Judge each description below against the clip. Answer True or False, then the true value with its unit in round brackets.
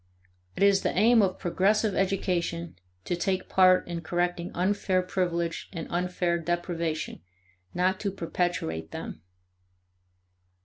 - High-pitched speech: False (180 Hz)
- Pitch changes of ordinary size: False (1.9 semitones)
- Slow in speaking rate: True (120 wpm)